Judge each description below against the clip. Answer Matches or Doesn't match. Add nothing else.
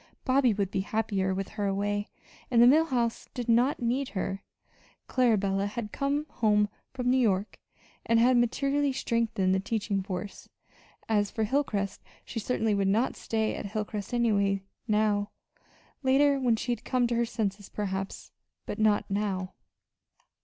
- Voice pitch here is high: Matches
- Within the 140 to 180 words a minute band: Matches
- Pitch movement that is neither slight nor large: Matches